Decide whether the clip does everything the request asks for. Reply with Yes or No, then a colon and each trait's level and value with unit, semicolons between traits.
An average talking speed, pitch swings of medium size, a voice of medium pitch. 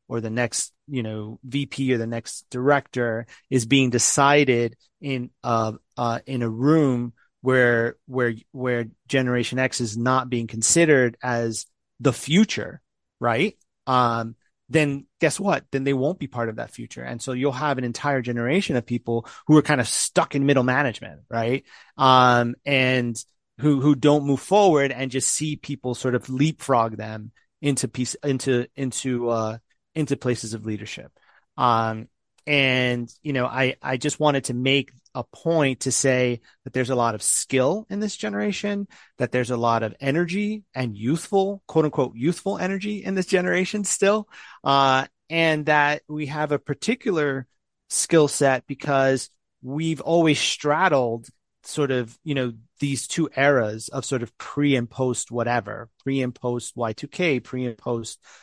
No: average, 165 wpm; average, 3.6 semitones; low, 130 Hz